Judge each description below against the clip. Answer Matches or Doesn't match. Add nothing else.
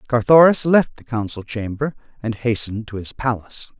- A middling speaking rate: Matches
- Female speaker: Doesn't match